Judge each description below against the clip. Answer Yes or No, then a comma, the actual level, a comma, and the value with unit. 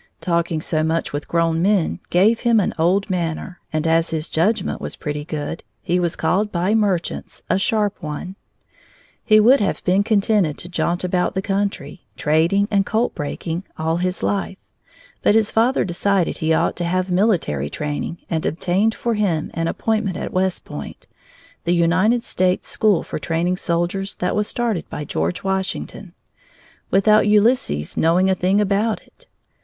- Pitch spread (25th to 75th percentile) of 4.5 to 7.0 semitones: No, average, 3.7 semitones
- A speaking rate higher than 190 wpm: No, average, 165 wpm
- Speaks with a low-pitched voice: No, medium, 185 Hz